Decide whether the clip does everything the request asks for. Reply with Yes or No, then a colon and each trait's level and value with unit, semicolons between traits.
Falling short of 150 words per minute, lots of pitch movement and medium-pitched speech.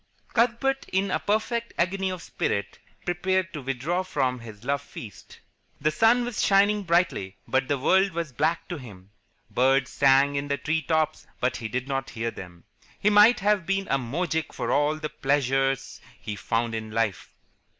No: average, 175 wpm; wide, 6.8 semitones; medium, 145 Hz